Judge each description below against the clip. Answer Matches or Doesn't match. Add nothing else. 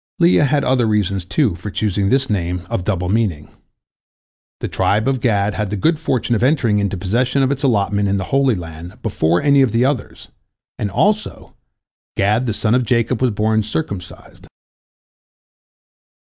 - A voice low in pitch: Matches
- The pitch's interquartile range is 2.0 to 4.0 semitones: Doesn't match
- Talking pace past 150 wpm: Matches